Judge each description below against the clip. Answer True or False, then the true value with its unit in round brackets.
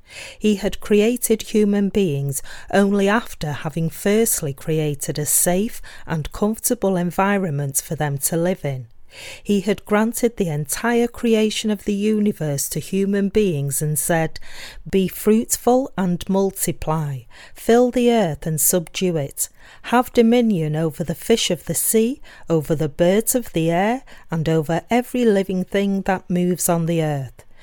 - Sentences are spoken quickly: False (150 wpm)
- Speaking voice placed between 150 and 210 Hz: True (185 Hz)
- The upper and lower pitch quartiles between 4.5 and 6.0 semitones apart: True (5.0 semitones)